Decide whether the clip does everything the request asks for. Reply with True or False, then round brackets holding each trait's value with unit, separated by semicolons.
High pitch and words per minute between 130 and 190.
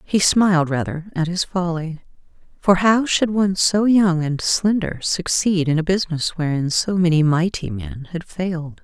False (175 Hz; 170 wpm)